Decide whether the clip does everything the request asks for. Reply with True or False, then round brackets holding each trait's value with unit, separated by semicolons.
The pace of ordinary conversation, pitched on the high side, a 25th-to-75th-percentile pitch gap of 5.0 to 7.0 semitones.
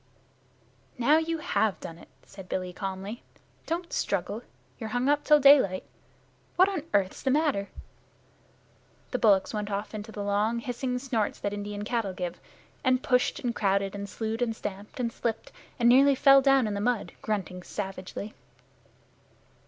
False (160 wpm; 220 Hz; 4.3 semitones)